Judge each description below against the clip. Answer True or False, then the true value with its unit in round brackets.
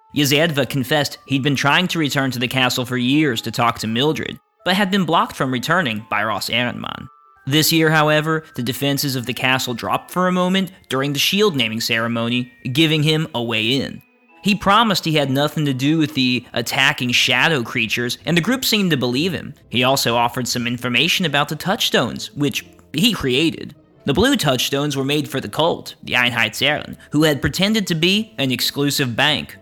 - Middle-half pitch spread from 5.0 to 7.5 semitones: False (4.2 semitones)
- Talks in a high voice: False (140 Hz)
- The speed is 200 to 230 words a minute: False (190 wpm)